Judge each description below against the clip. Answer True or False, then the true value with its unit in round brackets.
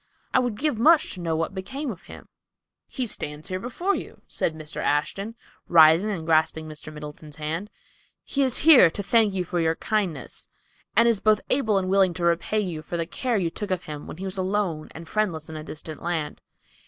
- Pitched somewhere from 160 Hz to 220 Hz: True (185 Hz)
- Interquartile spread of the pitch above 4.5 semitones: True (5.1 semitones)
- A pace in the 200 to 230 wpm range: True (205 wpm)